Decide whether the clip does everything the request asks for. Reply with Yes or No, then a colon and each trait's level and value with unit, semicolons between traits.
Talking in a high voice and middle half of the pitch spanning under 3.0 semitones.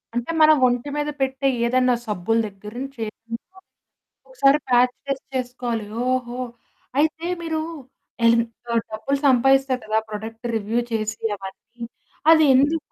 No: very high, 250 Hz; average, 3.4 semitones